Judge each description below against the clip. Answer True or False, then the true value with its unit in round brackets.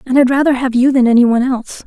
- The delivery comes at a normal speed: False (290 wpm)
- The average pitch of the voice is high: True (255 Hz)